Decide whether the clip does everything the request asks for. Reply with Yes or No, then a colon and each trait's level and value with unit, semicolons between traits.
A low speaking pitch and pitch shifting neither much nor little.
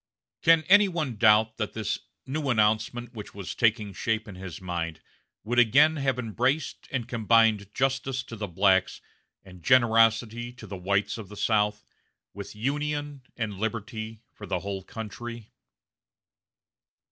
Yes: low, 110 Hz; average, 3.5 semitones